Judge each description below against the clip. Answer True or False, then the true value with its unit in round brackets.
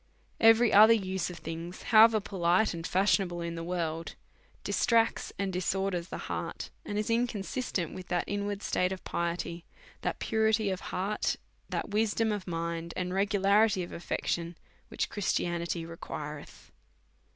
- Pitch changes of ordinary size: True (3.6 semitones)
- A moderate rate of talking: True (145 wpm)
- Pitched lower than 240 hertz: True (185 Hz)